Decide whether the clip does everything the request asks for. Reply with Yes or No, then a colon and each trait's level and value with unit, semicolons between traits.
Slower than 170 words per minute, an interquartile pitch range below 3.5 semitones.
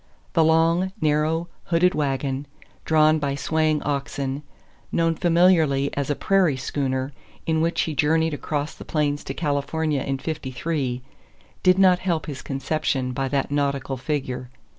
Yes: average, 140 wpm; average, 2.9 semitones